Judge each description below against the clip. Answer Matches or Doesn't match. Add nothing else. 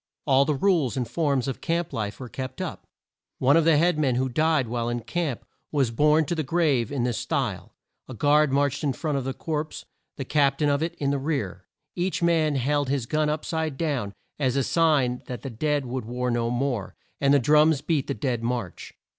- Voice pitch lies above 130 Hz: Matches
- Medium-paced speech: Doesn't match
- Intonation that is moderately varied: Matches